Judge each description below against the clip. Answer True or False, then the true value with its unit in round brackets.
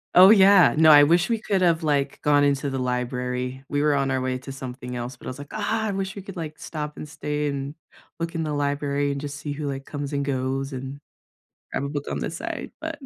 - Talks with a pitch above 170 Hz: False (145 Hz)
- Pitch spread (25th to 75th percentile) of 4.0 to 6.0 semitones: False (2.7 semitones)